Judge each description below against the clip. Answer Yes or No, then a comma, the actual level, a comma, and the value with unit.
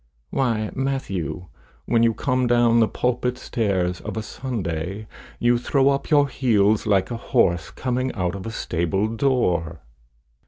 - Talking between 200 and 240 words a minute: No, average, 150 wpm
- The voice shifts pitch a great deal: No, average, 4.8 semitones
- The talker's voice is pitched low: Yes, low, 115 Hz